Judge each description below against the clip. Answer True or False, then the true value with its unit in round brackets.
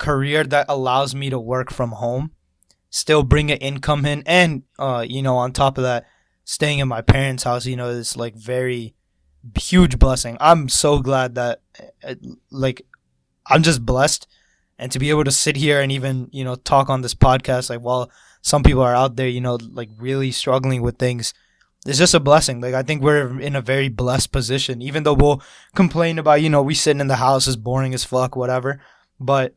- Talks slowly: False (205 wpm)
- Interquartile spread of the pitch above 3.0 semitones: False (2.4 semitones)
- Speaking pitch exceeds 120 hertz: True (130 Hz)